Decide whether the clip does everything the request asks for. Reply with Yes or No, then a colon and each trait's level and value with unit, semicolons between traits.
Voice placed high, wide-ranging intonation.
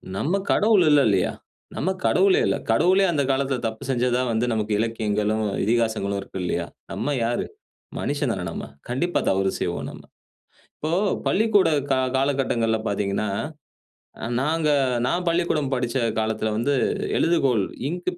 No: low, 125 Hz; wide, 6.8 semitones